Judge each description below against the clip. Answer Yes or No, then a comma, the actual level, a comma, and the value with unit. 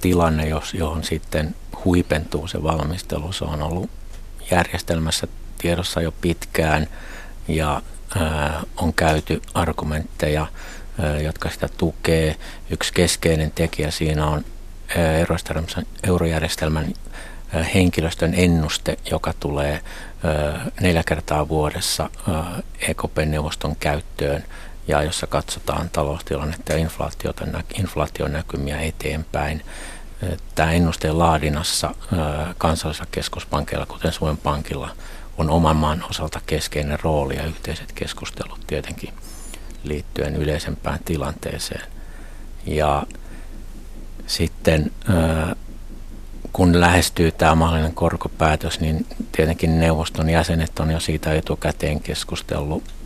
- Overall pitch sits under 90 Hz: Yes, very low, 80 Hz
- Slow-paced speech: Yes, slow, 90 wpm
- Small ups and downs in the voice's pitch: Yes, narrow, 1.8 semitones